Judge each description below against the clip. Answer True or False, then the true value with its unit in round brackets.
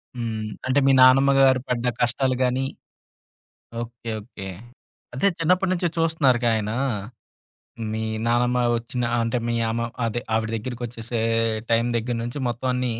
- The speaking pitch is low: True (120 Hz)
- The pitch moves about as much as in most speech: False (2.1 semitones)